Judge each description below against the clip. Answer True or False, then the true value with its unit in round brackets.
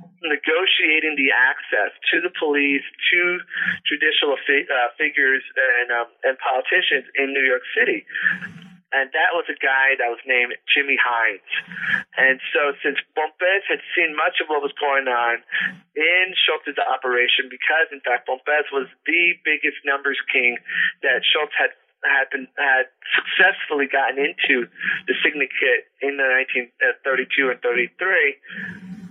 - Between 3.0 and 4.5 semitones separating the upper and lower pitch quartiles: False (5.4 semitones)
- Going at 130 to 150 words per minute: True (145 wpm)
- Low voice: False (155 Hz)